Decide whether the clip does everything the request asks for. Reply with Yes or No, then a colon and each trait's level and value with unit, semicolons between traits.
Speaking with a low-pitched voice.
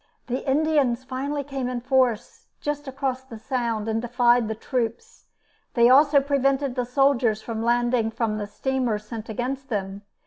No: very high, 250 Hz